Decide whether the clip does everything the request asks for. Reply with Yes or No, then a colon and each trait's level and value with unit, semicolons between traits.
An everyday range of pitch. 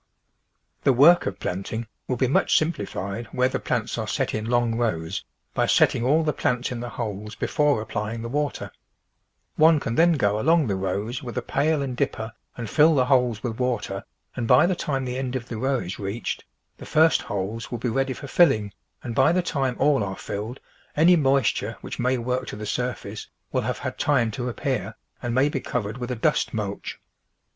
Yes: average, 3.9 semitones